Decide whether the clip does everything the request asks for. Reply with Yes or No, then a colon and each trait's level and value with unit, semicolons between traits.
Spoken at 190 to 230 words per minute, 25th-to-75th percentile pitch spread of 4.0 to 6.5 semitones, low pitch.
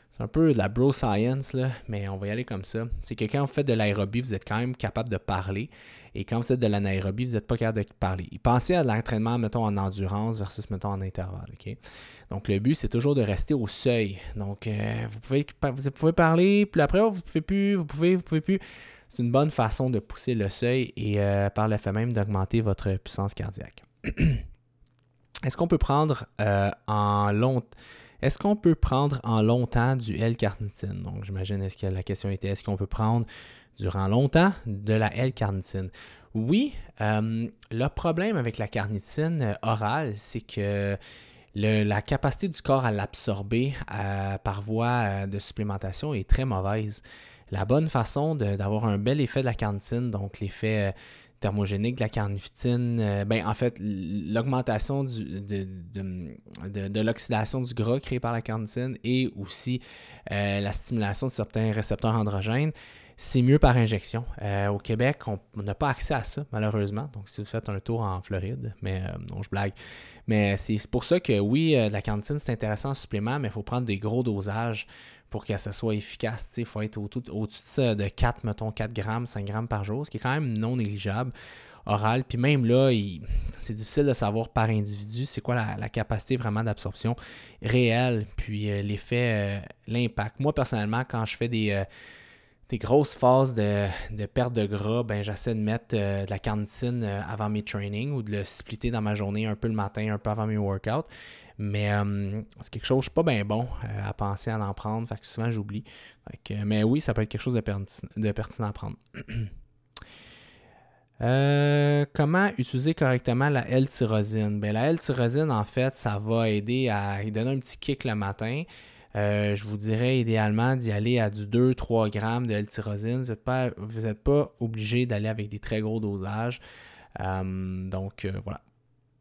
No: average, 200 wpm; average, 3.4 semitones; low, 110 Hz